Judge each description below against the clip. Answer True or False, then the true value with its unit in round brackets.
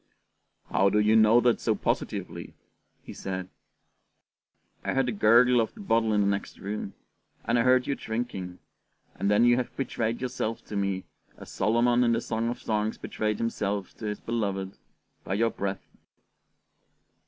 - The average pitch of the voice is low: True (110 Hz)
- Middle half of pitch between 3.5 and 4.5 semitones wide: False (3.0 semitones)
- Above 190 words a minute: False (165 wpm)